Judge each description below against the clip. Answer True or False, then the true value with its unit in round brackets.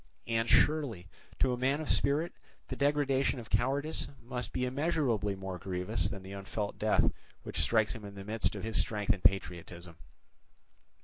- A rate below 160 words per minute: False (170 wpm)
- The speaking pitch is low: True (115 Hz)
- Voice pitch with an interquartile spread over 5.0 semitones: True (5.6 semitones)